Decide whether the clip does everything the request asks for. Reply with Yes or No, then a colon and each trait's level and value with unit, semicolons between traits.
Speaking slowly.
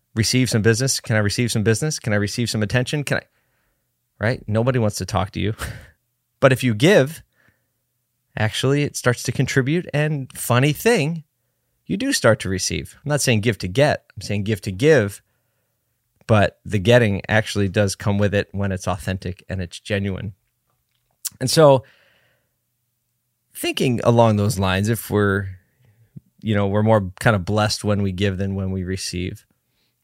No: average, 170 wpm